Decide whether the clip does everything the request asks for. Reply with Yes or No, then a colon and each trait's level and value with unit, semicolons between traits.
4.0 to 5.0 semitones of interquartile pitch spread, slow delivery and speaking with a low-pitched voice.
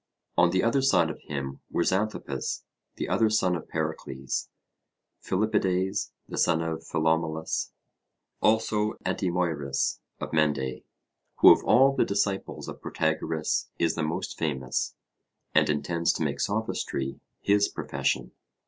Yes: average, 4.7 semitones; slow, 130 wpm; very low, 80 Hz